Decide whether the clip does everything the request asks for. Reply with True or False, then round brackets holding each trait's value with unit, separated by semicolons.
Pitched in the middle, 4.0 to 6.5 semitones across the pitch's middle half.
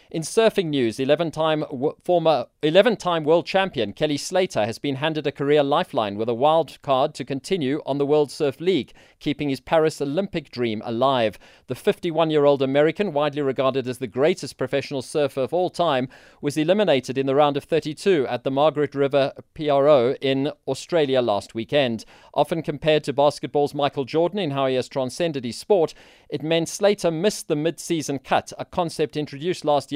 False (145 Hz; 3.2 semitones)